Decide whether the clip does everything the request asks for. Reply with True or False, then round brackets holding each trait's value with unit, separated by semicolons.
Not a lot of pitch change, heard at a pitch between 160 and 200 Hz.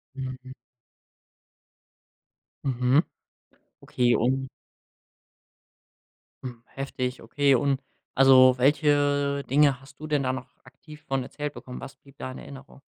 False (1.7 semitones; 135 Hz)